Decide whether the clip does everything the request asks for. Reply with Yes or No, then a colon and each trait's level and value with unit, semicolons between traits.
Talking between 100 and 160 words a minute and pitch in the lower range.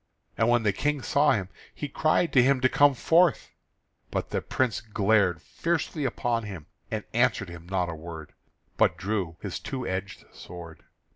No: average, 170 wpm; low, 110 Hz